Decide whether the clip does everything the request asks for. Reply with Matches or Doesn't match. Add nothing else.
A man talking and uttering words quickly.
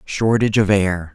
Doesn't match